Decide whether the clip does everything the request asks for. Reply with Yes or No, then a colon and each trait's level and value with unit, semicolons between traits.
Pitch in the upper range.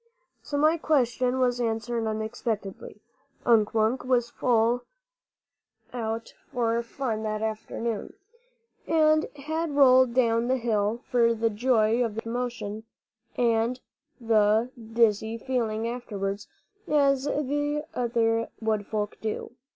Yes: high, 235 Hz